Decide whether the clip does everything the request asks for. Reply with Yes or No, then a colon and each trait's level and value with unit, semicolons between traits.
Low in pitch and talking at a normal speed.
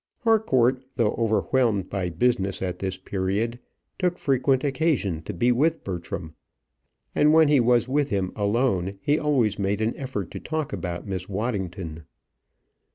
Yes: low, 110 Hz; average, 150 wpm